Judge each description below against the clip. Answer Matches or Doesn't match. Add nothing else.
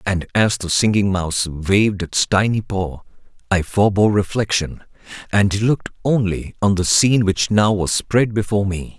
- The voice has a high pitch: Doesn't match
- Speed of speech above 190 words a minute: Doesn't match